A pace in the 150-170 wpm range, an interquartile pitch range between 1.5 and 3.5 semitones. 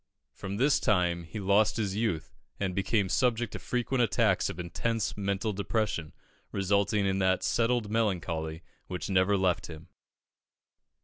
No: average, 140 wpm; average, 3.1 semitones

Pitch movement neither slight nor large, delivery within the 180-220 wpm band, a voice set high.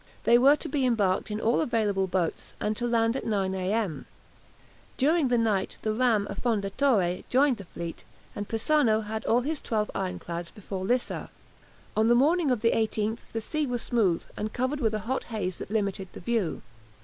Yes: average, 3.8 semitones; average, 185 wpm; high, 220 Hz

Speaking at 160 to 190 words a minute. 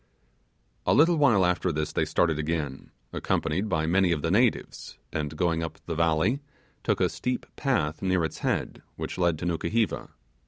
Yes: average, 170 wpm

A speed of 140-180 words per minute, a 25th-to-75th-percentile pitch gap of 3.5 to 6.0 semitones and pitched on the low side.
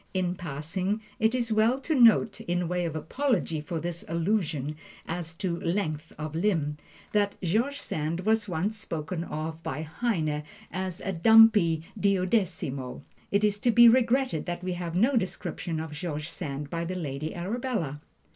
No: average, 160 wpm; average, 5.1 semitones; medium, 175 Hz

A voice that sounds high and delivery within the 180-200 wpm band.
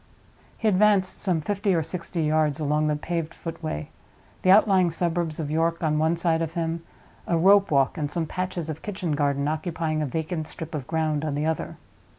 No: medium, 160 Hz; average, 190 wpm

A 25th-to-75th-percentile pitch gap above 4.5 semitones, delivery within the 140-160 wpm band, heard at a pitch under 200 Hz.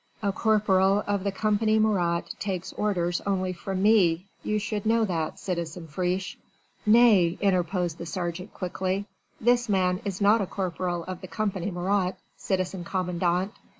No: narrow, 2.6 semitones; average, 150 wpm; high, 190 Hz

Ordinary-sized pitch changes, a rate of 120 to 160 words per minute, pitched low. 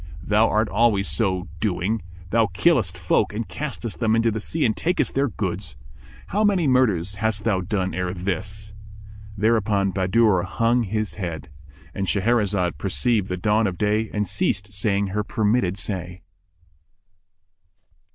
Yes: average, 3.2 semitones; average, 140 wpm; low, 105 Hz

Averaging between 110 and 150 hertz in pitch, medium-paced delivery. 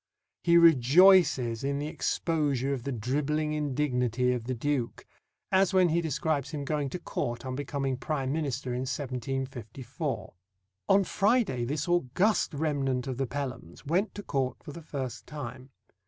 Yes: medium, 140 Hz; average, 155 wpm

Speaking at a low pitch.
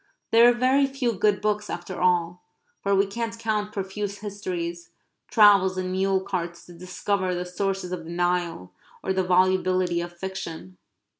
No: high, 190 Hz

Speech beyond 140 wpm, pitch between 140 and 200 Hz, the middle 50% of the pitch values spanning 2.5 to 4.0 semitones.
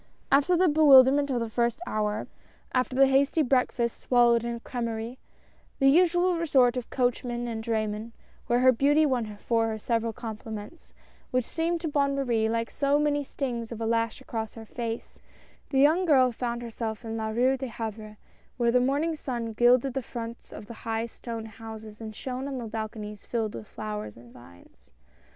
No: average, 190 wpm; high, 235 Hz; average, 3.3 semitones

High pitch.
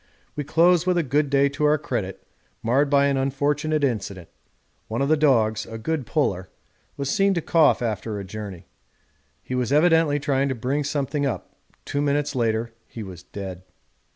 No: medium, 140 Hz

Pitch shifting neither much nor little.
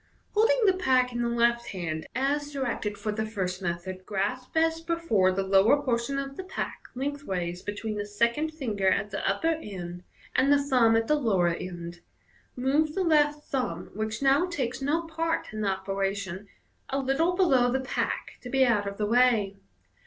No: wide, 6.4 semitones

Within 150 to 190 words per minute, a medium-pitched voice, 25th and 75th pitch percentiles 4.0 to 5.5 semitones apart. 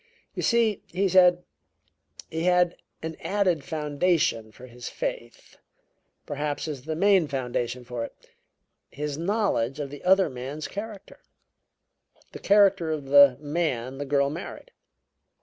No: slow, 135 wpm; medium, 155 Hz; average, 5.1 semitones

